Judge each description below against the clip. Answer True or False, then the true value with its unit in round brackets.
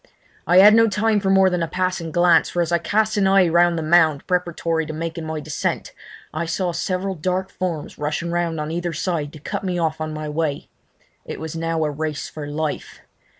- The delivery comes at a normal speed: False (215 wpm)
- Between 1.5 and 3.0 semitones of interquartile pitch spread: True (2.7 semitones)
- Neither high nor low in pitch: True (170 Hz)